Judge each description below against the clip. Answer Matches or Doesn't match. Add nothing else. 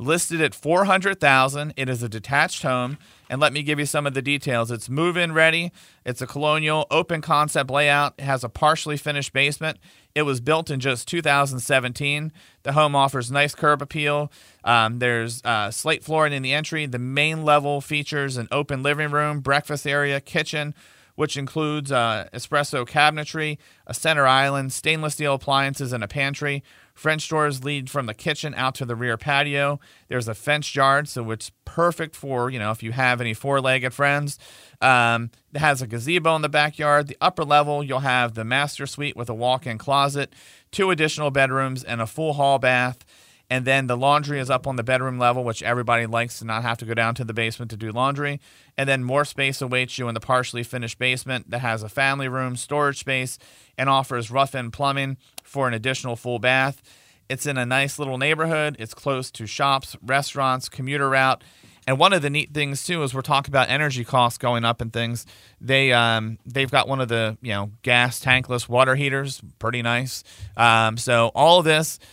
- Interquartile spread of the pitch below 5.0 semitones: Matches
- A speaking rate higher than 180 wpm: Matches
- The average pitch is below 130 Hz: Doesn't match